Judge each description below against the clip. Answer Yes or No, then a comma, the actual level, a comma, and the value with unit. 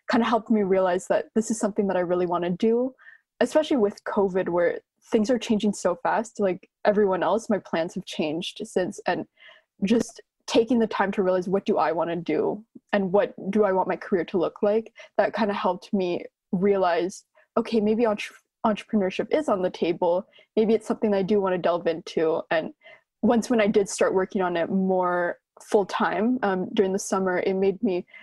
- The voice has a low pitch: No, high, 205 Hz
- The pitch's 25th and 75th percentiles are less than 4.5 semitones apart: Yes, average, 3.3 semitones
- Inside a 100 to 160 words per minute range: No, fast, 205 wpm